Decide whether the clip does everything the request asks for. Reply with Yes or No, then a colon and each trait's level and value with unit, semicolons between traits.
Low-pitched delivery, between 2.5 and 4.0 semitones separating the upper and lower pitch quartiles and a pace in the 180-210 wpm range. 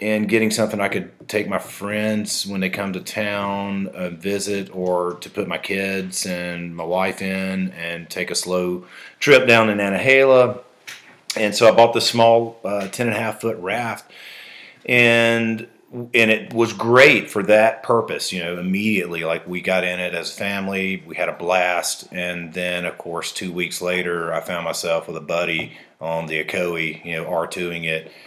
Yes: very low, 95 Hz; average, 3.4 semitones; average, 185 wpm